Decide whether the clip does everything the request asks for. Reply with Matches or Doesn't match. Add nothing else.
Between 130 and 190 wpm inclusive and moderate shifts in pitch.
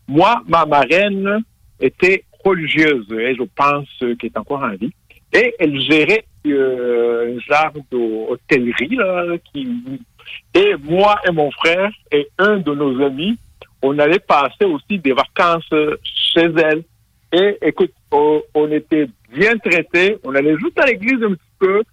Doesn't match